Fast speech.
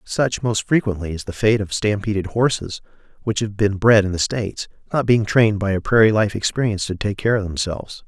Yes: fast, 215 wpm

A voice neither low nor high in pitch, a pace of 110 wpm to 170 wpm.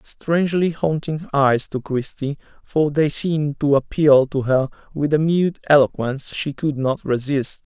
Yes: medium, 145 Hz; average, 155 wpm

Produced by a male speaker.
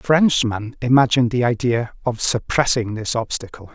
Yes: male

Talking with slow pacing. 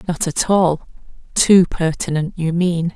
Yes: slow, 120 wpm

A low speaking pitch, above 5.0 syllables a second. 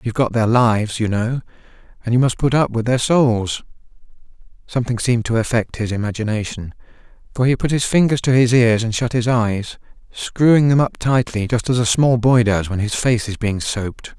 Yes: low, 120 Hz; 5.4 syllables/s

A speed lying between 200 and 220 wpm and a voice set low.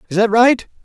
No: fast, 215 wpm; high, 225 Hz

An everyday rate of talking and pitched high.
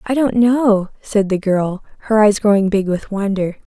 Yes: average, 195 wpm; high, 205 Hz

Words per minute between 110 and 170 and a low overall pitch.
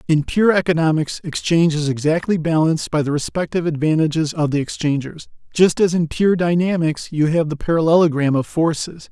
No: average, 165 wpm; medium, 160 Hz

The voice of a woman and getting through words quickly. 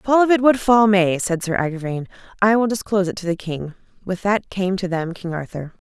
Yes: female; fast, 235 wpm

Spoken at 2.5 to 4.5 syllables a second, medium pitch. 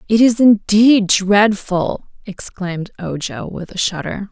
No: 3.9 syllables/s; high, 205 Hz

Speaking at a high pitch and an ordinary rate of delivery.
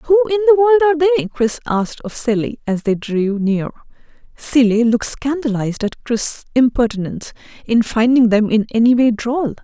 Yes: very high, 255 Hz; average, 170 wpm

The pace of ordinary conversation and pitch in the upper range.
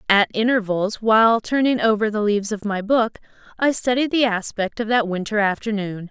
Yes: average, 175 wpm; high, 215 Hz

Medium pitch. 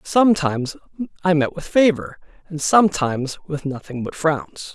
Yes: medium, 160 Hz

